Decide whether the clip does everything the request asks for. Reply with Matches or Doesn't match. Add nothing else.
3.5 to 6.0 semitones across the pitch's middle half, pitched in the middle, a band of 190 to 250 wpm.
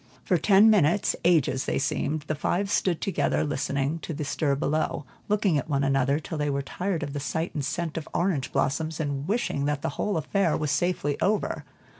Matches